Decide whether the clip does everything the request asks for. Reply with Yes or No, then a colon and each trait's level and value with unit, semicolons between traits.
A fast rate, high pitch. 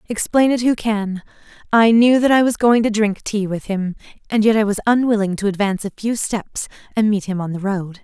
Yes: fast, 225 wpm; high, 210 Hz